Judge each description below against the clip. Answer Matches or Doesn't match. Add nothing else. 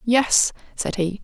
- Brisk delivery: Doesn't match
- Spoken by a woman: Matches